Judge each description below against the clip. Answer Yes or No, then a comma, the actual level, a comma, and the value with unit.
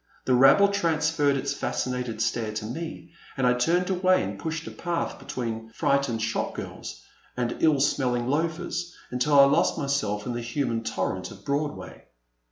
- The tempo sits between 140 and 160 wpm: No, average, 170 wpm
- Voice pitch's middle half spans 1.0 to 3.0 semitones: No, average, 5.1 semitones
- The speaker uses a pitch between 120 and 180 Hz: Yes, medium, 140 Hz